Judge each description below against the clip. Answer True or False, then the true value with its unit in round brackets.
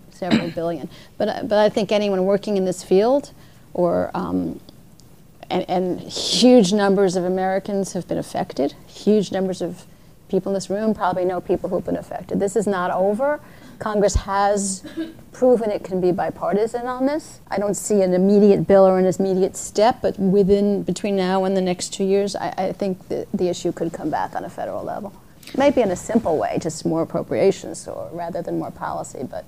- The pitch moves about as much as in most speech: False (2.2 semitones)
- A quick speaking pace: False (190 wpm)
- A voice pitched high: True (195 Hz)